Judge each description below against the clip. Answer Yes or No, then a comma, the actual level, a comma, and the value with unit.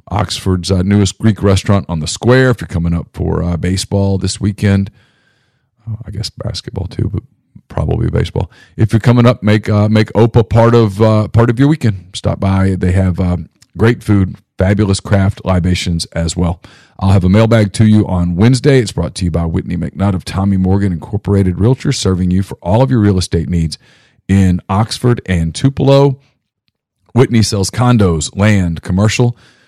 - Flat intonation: No, average, 3.7 semitones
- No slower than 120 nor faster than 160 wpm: No, average, 185 wpm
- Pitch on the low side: Yes, low, 100 Hz